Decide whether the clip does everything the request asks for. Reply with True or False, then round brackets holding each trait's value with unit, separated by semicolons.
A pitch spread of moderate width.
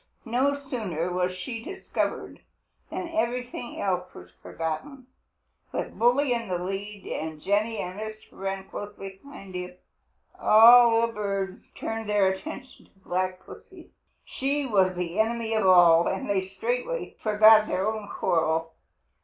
True (4.1 semitones)